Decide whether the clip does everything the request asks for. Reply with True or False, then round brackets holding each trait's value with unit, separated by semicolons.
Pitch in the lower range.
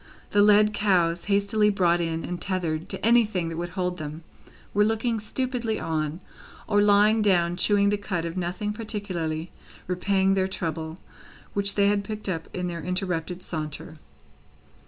False (185 Hz)